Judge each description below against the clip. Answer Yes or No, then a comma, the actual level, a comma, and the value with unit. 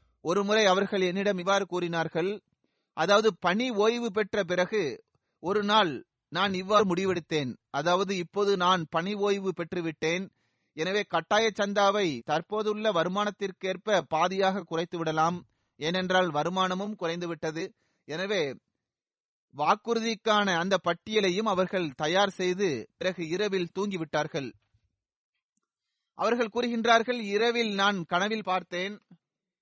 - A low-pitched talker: No, high, 190 Hz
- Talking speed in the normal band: Yes, average, 95 wpm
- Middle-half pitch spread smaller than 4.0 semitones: Yes, average, 3.5 semitones